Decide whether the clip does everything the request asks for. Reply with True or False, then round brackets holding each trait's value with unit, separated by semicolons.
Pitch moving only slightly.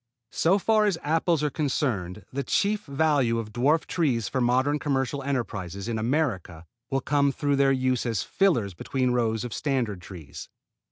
False (4.6 semitones)